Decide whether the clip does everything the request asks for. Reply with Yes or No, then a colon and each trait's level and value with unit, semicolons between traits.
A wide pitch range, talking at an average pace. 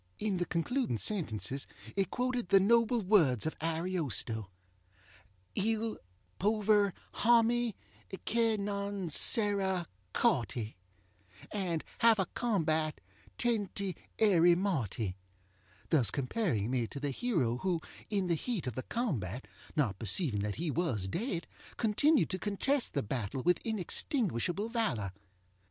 No: wide, 8.2 semitones; slow, 120 wpm